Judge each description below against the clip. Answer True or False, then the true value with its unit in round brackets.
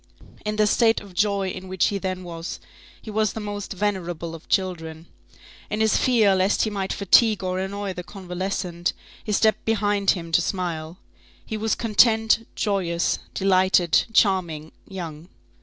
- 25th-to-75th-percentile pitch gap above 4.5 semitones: False (2.9 semitones)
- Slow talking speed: False (155 wpm)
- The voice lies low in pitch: False (190 Hz)